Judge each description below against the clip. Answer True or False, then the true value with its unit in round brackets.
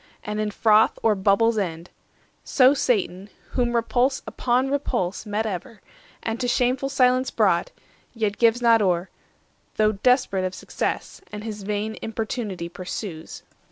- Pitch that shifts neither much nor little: True (3.6 semitones)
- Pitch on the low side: False (220 Hz)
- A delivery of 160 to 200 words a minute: False (145 wpm)